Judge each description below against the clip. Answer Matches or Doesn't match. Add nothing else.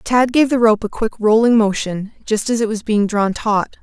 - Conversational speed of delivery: Doesn't match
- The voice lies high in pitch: Matches